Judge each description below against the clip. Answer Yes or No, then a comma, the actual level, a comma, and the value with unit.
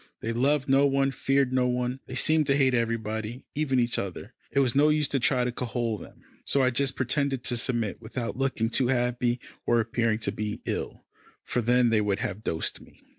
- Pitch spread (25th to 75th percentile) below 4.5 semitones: Yes, average, 2.8 semitones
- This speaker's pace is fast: Yes, fast, 215 wpm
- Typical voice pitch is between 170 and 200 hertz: No, low, 125 Hz